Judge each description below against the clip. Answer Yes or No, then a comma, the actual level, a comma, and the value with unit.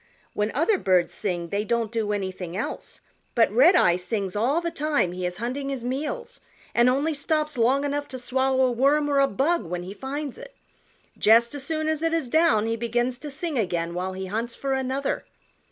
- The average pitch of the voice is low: No, very high, 250 Hz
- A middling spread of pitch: No, wide, 5.7 semitones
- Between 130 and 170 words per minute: No, average, 200 wpm